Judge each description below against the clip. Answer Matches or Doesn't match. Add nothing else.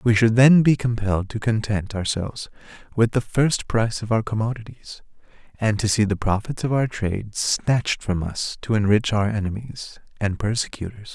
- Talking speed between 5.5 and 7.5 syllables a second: Doesn't match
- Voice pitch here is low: Matches